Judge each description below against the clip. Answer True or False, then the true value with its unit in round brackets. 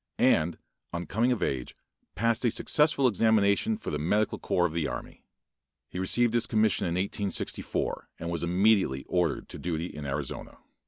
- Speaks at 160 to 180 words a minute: True (165 wpm)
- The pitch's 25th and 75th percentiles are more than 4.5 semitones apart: True (5.0 semitones)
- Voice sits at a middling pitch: False (95 Hz)